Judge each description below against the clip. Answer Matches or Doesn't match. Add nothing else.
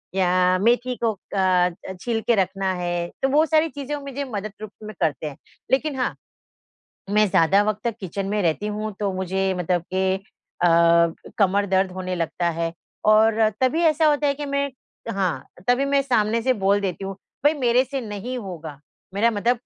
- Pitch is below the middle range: Doesn't match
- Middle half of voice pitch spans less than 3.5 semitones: Doesn't match